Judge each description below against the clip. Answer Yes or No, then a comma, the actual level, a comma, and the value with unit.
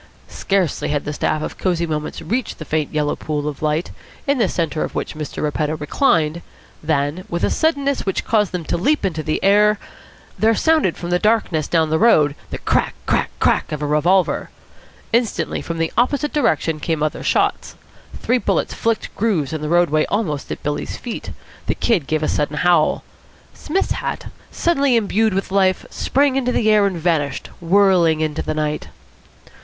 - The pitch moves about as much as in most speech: No, wide, 6.0 semitones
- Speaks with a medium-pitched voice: Yes, medium, 170 Hz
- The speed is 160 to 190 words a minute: Yes, average, 180 wpm